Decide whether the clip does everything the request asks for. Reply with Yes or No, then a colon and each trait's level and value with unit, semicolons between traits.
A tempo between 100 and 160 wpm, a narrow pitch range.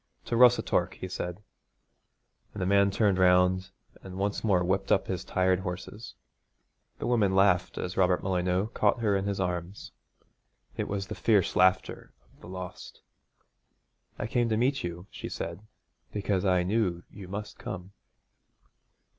Yes: average, 155 wpm; narrow, 2.0 semitones